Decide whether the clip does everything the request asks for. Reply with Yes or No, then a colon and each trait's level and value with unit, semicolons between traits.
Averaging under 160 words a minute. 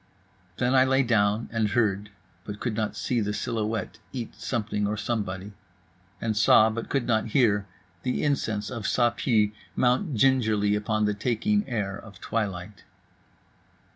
Yes: average, 150 wpm